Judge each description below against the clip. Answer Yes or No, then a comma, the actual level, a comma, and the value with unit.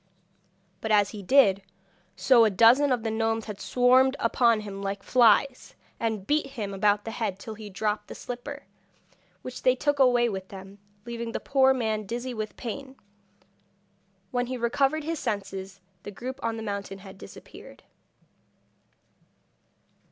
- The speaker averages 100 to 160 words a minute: Yes, average, 155 wpm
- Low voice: No, high, 225 Hz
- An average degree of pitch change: Yes, average, 3.7 semitones